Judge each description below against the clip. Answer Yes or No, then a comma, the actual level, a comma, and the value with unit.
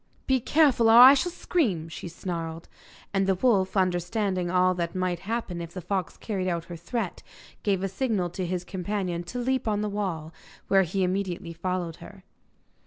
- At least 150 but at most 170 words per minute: No, average, 180 wpm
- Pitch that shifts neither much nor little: Yes, average, 3.2 semitones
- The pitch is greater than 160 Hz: Yes, medium, 185 Hz